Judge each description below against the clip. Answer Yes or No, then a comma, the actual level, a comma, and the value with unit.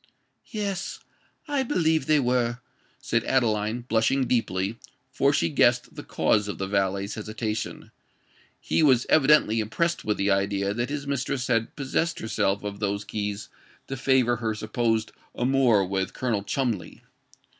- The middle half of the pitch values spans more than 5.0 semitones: No, average, 4.5 semitones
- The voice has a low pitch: Yes, low, 115 Hz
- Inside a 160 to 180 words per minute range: No, slow, 135 wpm